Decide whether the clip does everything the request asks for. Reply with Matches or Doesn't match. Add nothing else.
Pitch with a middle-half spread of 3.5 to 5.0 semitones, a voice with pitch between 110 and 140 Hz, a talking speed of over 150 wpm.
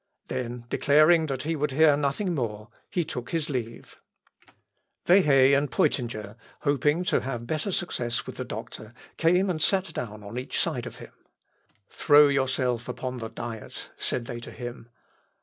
Matches